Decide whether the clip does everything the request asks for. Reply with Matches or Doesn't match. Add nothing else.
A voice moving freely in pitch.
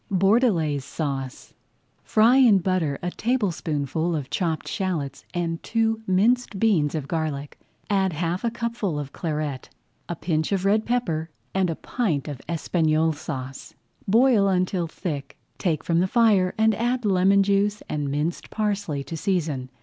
Doesn't match